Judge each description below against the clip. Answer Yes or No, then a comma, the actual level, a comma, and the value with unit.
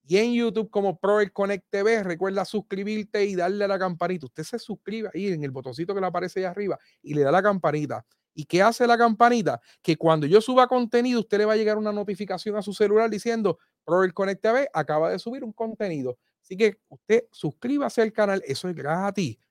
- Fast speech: Yes, fast, 220 wpm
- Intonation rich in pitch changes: No, average, 3.7 semitones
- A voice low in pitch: No, high, 200 Hz